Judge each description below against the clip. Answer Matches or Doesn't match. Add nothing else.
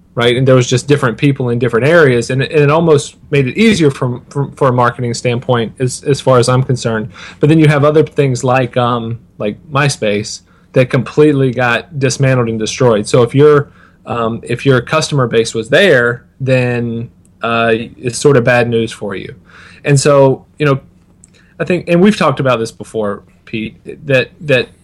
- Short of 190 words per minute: Doesn't match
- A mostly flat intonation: Doesn't match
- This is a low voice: Matches